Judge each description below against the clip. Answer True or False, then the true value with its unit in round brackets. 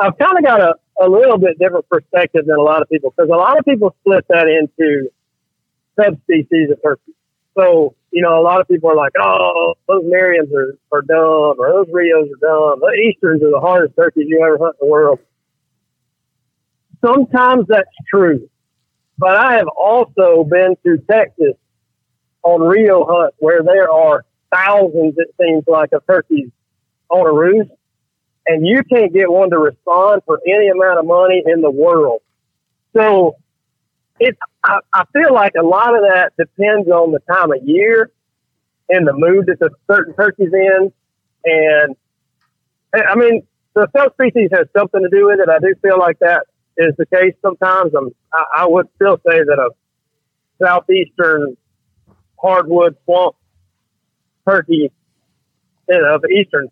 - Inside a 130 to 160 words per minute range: False (170 wpm)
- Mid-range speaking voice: True (180 Hz)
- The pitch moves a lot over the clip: False (4.7 semitones)